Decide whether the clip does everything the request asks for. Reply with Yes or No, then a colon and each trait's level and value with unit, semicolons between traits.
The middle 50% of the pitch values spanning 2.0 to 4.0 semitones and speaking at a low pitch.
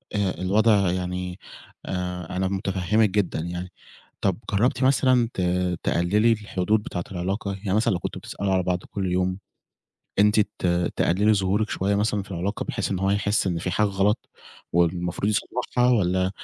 Yes: narrow, 2.5 semitones; very low, 95 Hz